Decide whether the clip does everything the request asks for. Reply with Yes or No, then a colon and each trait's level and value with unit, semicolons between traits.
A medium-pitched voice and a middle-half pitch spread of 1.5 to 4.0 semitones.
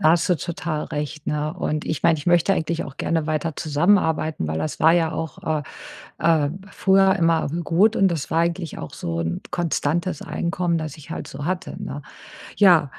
Yes: medium, 160 Hz; narrow, 2.4 semitones